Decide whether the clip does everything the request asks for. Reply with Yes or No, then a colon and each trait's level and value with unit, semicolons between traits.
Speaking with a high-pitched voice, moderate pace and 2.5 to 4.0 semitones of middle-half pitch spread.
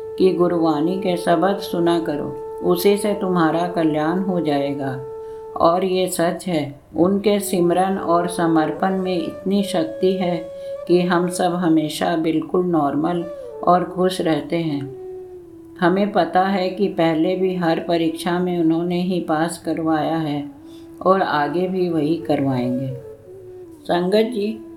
No: medium, 175 Hz; average, 135 wpm; average, 2.9 semitones